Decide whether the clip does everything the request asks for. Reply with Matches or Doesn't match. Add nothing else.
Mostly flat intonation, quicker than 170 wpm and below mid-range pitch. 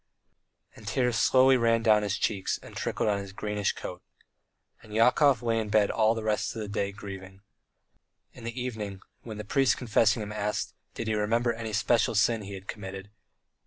Matches